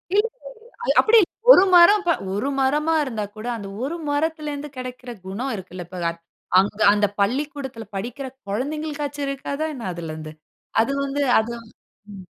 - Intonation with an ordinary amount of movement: No, wide, 6.3 semitones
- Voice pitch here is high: Yes, very high, 265 Hz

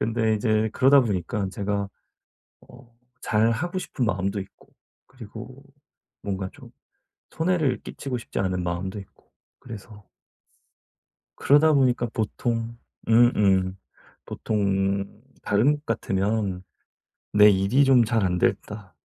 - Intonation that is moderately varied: Yes, average, 3.8 semitones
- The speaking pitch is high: No, low, 110 Hz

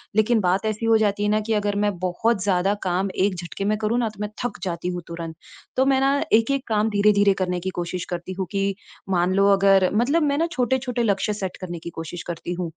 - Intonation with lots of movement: No, average, 3.4 semitones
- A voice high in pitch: Yes, high, 200 Hz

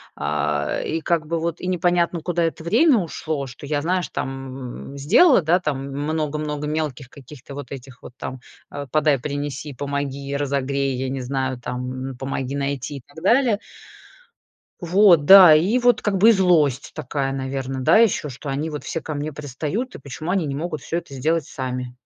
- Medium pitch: Yes, medium, 145 Hz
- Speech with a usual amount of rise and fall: Yes, average, 3.8 semitones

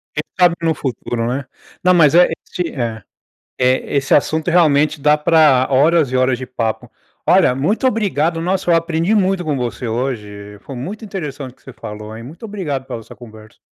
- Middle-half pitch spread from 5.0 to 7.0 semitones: Yes, wide, 5.5 semitones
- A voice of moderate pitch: Yes, medium, 145 Hz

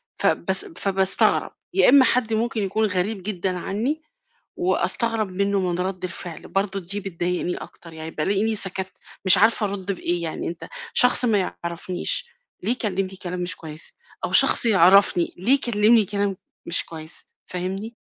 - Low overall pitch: No, high, 195 Hz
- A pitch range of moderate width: Yes, average, 3.3 semitones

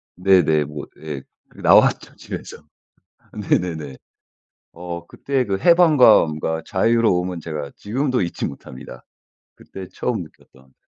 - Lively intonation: Yes, wide, 5.7 semitones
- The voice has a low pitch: Yes, very low, 90 Hz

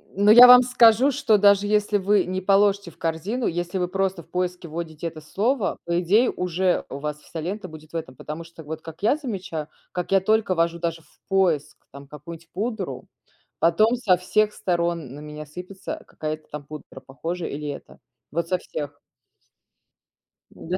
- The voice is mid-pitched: Yes, medium, 175 Hz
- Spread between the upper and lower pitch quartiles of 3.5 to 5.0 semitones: Yes, average, 4.2 semitones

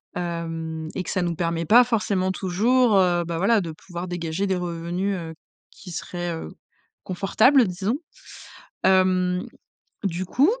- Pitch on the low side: No, medium, 180 Hz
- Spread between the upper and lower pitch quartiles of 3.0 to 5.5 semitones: No, narrow, 2.5 semitones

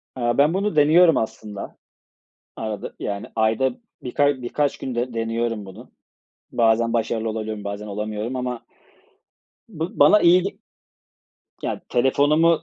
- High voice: No, low, 120 Hz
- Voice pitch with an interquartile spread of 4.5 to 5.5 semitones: Yes, average, 4.8 semitones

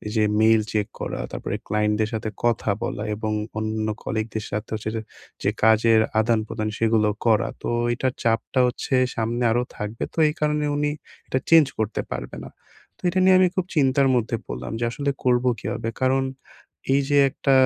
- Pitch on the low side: Yes, low, 115 Hz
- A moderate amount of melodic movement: Yes, average, 3.2 semitones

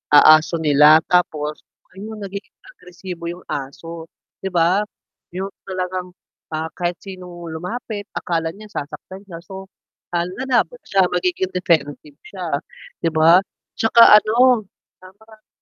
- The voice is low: No, medium, 180 Hz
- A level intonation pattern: No, average, 3.5 semitones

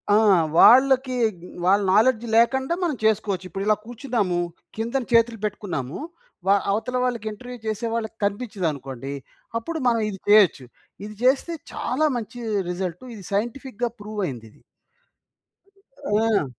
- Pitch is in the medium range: No, high, 220 Hz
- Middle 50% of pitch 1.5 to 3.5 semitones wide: No, average, 3.9 semitones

